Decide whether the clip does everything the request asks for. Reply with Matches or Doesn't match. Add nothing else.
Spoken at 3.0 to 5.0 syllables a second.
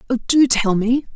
Matches